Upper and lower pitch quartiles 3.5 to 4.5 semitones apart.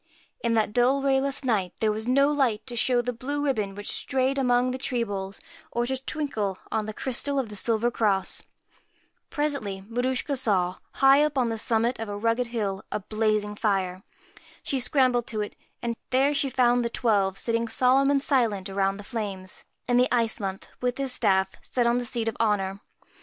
Yes: average, 3.8 semitones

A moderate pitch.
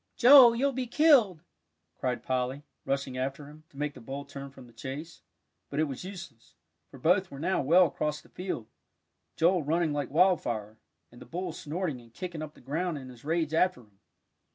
Yes: medium, 150 Hz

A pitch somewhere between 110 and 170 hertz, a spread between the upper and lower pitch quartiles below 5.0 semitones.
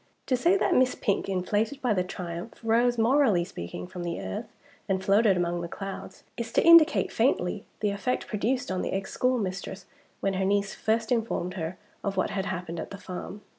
No: high, 200 Hz; average, 4.1 semitones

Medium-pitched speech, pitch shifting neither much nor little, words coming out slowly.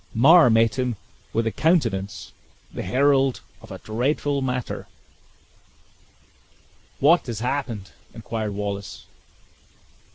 No: low, 120 Hz; average, 4.4 semitones; slow, 100 wpm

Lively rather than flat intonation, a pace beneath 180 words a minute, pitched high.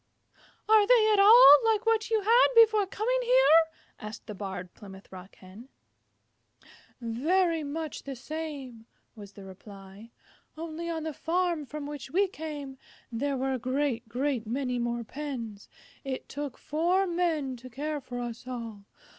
Yes: wide, 6.6 semitones; average, 155 wpm; very high, 285 Hz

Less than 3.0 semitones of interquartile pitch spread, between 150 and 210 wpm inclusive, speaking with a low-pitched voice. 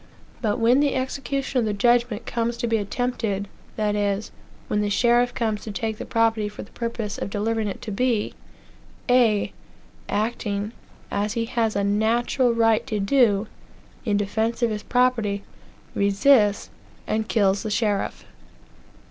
No: narrow, 2.5 semitones; average, 155 wpm; high, 220 Hz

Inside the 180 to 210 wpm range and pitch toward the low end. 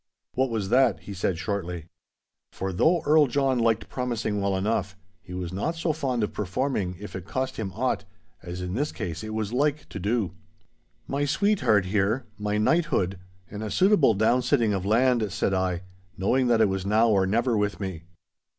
Yes: average, 185 wpm; low, 110 Hz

